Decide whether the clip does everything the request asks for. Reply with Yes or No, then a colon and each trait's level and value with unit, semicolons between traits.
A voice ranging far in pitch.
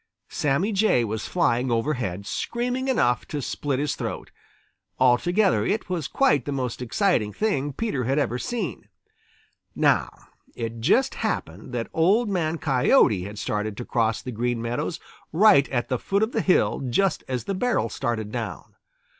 Yes: wide, 8.7 semitones